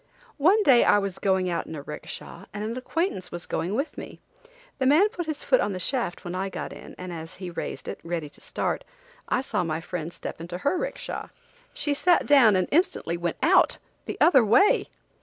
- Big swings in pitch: Yes, wide, 8.7 semitones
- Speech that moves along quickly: Yes, fast, 210 wpm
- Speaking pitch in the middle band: No, high, 200 Hz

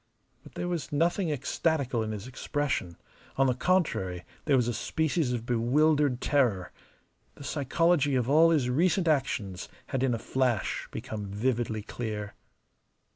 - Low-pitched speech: Yes, low, 130 Hz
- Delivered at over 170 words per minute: No, average, 145 wpm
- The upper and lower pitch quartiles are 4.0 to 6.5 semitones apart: Yes, average, 5.1 semitones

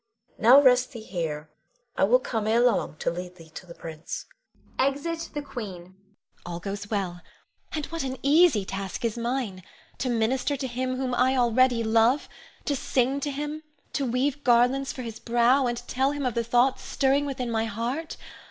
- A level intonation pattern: No, average, 3.7 semitones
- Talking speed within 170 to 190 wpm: Yes, average, 180 wpm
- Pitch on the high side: Yes, high, 245 Hz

